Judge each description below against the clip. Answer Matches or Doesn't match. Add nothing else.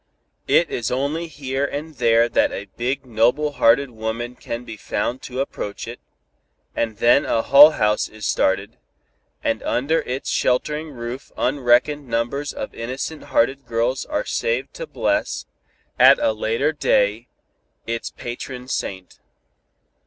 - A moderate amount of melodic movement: Matches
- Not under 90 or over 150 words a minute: Matches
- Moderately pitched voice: Doesn't match